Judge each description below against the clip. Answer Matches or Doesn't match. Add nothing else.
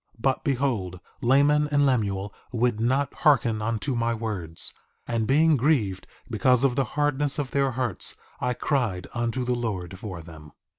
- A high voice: Doesn't match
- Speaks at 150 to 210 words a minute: Matches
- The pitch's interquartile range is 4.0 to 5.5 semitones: Matches